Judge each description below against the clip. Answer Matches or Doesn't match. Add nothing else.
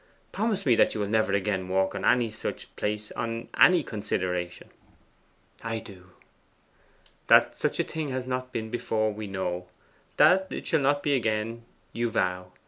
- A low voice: Matches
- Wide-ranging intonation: Doesn't match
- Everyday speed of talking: Matches